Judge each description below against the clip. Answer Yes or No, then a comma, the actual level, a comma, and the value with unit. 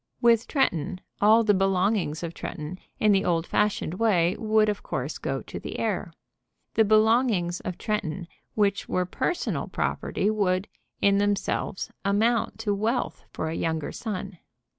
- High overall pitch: Yes, high, 200 Hz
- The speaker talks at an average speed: Yes, average, 150 wpm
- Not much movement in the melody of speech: No, average, 3.2 semitones